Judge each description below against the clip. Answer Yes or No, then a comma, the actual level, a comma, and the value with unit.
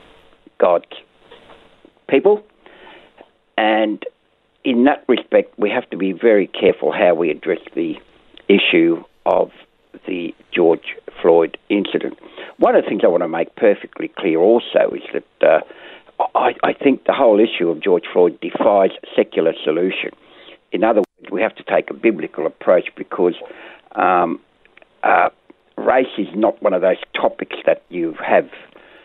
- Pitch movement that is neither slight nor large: No, wide, 5.9 semitones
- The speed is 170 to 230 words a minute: No, average, 145 wpm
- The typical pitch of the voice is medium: No, very high, 390 Hz